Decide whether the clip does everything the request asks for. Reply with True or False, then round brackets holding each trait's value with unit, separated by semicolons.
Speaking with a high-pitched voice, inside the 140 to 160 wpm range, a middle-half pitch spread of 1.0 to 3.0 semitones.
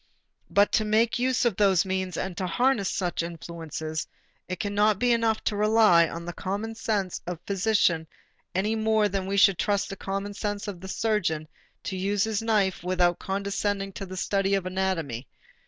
False (195 Hz; 185 wpm; 2.6 semitones)